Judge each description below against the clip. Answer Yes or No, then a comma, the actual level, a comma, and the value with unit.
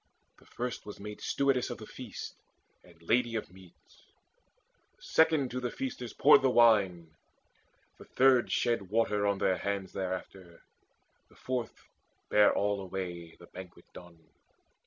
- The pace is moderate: Yes, average, 145 wpm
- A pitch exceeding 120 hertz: No, low, 100 Hz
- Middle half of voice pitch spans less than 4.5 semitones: No, average, 4.9 semitones